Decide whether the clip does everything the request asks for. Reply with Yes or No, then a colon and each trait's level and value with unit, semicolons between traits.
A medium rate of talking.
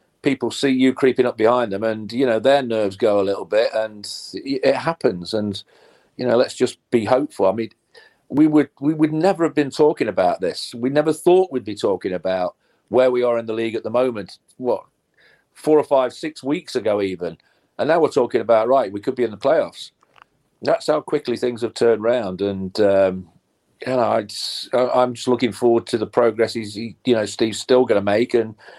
No: fast, 215 wpm